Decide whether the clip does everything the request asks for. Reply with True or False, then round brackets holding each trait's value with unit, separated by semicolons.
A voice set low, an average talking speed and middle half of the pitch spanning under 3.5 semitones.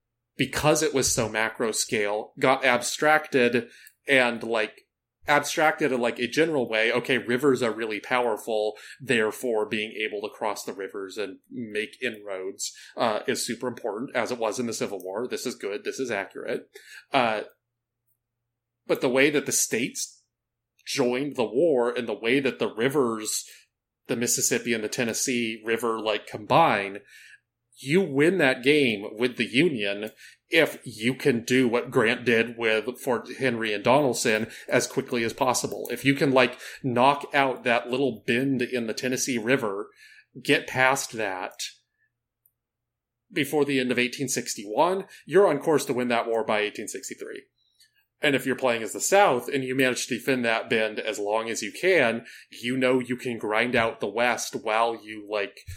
True (120 Hz; 165 wpm; 3.1 semitones)